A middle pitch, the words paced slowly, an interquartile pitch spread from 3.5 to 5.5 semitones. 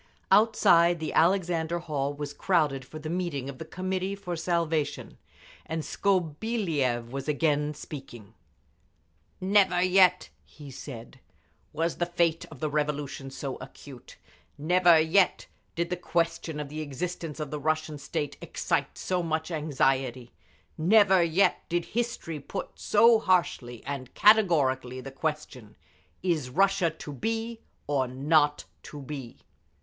Yes: medium, 160 Hz; slow, 130 wpm; average, 4.0 semitones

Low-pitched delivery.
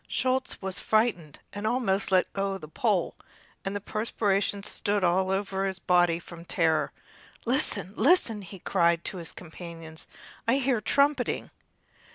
No: high, 195 Hz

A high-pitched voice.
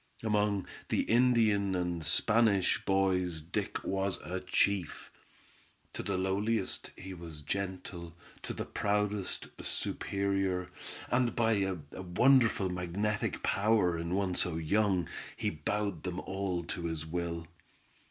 No: very low, 95 Hz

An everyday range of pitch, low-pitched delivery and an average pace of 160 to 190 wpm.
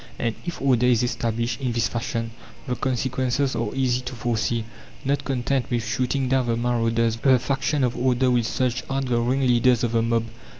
No: narrow, 1.9 semitones; low, 125 Hz; average, 185 wpm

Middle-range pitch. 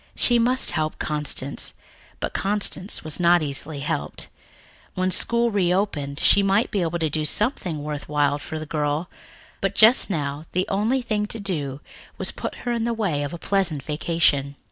Yes: medium, 170 Hz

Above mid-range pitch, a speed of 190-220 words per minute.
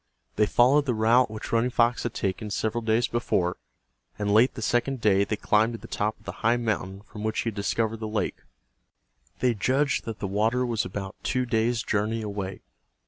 No: low, 110 Hz; average, 200 wpm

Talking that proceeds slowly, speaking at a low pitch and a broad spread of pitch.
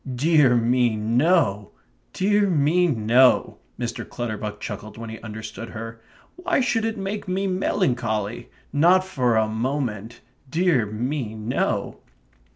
Yes: slow, 125 wpm; low, 125 Hz; wide, 8.0 semitones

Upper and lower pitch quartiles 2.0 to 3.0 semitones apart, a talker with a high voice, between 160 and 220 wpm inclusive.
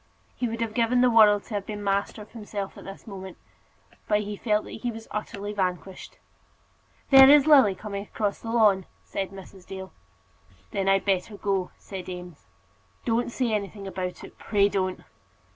Yes: narrow, 2.5 semitones; high, 205 Hz; average, 175 wpm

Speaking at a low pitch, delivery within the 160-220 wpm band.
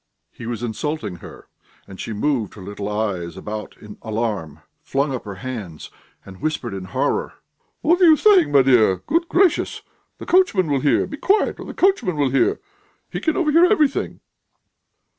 Yes: low, 130 Hz; average, 175 wpm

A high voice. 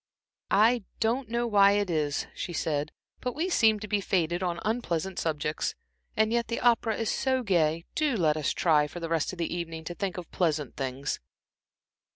No: medium, 180 Hz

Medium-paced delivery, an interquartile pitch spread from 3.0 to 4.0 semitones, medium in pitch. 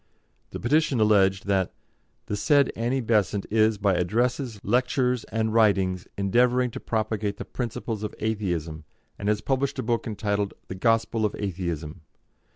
No: average, 150 wpm; average, 3.3 semitones; low, 110 Hz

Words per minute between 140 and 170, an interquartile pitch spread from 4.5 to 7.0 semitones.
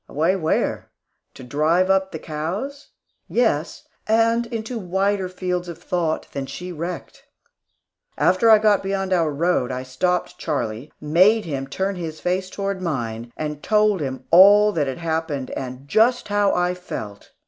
Yes: average, 160 wpm; average, 4.8 semitones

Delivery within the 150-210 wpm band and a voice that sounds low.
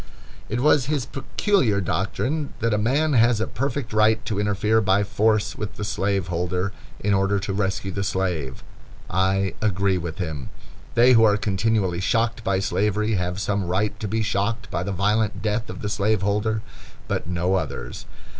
Yes: average, 170 wpm; low, 105 Hz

